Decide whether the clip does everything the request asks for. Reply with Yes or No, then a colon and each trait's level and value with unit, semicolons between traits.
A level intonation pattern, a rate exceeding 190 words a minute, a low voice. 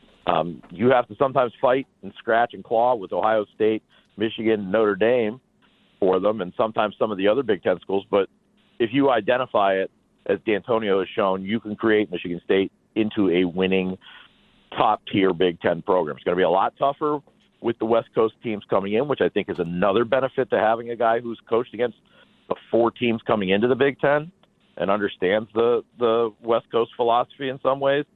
No: average, 4.0 semitones; average, 200 wpm; low, 115 Hz